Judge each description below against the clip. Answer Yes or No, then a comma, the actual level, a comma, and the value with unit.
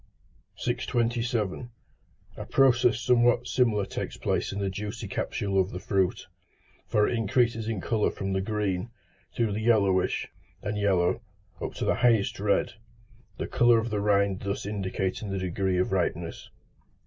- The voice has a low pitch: Yes, low, 105 Hz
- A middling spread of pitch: Yes, average, 3.3 semitones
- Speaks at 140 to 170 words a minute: Yes, average, 150 wpm